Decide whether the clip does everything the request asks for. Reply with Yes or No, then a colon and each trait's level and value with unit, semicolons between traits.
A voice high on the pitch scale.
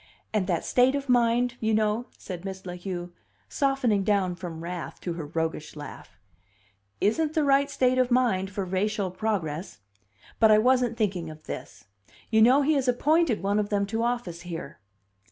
Yes: high, 210 Hz